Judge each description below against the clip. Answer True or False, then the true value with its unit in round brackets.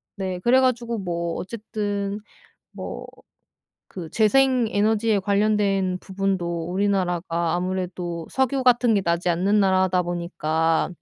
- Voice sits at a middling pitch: False (195 Hz)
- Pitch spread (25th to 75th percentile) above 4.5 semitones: False (3.5 semitones)